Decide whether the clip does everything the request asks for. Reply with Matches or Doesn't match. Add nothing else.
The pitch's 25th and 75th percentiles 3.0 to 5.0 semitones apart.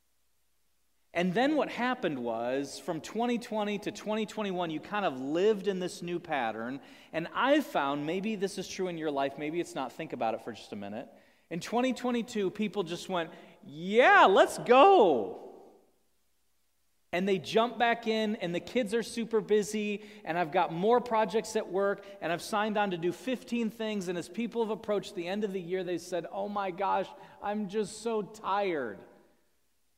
Matches